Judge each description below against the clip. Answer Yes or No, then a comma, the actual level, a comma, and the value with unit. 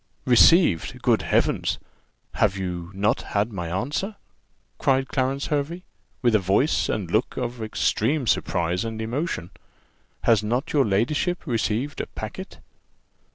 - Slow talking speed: Yes, slow, 130 wpm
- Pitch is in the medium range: No, low, 115 Hz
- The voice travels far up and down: Yes, wide, 5.9 semitones